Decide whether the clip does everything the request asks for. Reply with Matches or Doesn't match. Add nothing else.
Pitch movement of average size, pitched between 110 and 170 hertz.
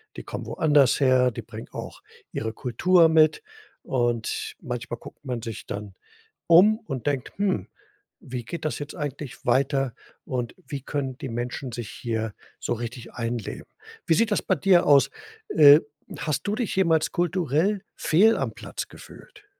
Doesn't match